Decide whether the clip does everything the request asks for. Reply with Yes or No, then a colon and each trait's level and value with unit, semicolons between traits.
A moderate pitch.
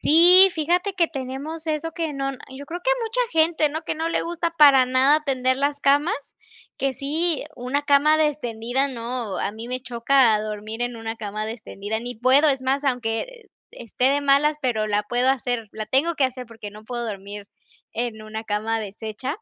No: very high, 260 Hz